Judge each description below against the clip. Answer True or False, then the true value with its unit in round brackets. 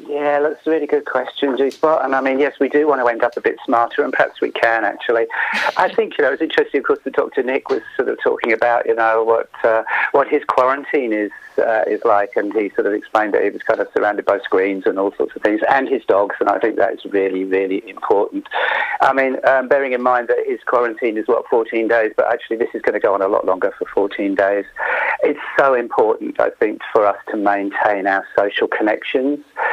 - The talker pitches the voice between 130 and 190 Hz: True (140 Hz)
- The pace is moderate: False (240 wpm)